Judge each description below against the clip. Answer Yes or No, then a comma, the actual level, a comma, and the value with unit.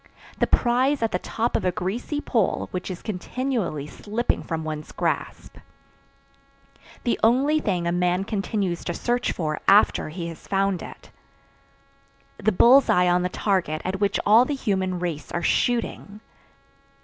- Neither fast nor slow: Yes, average, 155 wpm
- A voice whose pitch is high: Yes, high, 195 Hz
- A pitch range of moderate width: Yes, average, 5.0 semitones